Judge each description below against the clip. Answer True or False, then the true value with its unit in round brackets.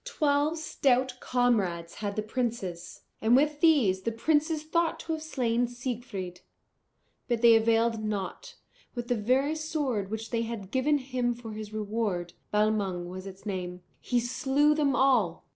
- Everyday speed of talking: True (155 wpm)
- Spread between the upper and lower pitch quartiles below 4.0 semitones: False (4.7 semitones)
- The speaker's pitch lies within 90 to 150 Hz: False (235 Hz)